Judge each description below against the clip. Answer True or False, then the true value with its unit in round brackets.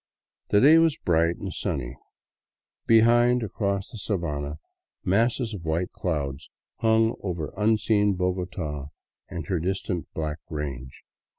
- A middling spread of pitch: False (5.9 semitones)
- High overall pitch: False (90 Hz)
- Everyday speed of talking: False (120 wpm)